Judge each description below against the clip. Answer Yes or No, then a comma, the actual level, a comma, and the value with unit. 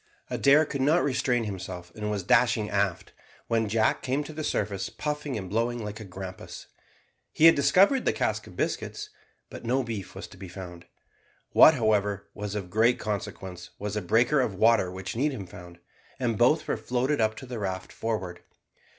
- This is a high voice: No, low, 110 Hz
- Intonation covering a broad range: No, average, 5.0 semitones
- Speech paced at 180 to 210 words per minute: Yes, average, 185 wpm